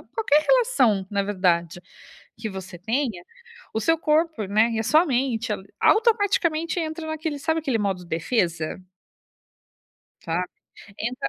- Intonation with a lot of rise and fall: Yes, wide, 8.6 semitones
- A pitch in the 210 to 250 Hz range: Yes, high, 235 Hz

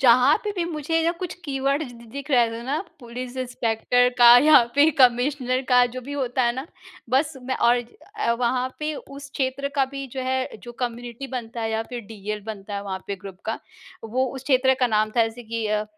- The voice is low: No, very high, 250 Hz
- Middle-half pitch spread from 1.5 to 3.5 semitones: Yes, average, 2.9 semitones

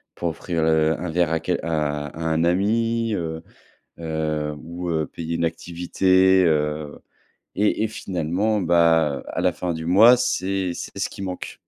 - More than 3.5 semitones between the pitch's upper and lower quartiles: No, average, 2.8 semitones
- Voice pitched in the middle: No, very low, 85 Hz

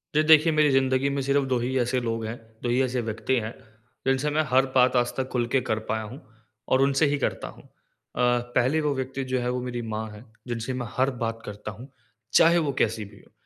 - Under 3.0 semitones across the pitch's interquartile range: Yes, narrow, 2.6 semitones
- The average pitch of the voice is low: Yes, low, 125 Hz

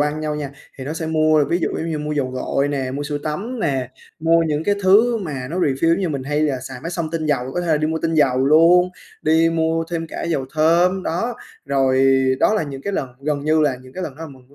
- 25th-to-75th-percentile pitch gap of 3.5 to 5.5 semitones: No, average, 3.1 semitones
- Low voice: No, medium, 155 Hz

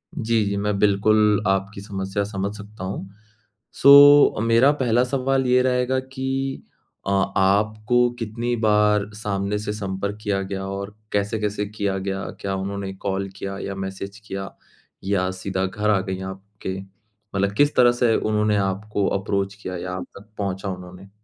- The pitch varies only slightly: Yes, narrow, 2.0 semitones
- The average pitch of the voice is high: No, low, 100 Hz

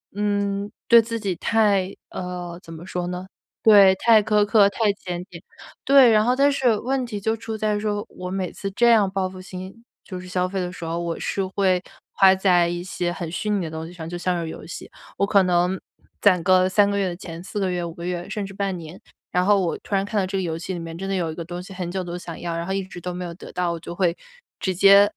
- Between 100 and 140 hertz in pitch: No, medium, 185 Hz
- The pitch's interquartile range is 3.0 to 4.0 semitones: No, narrow, 2.5 semitones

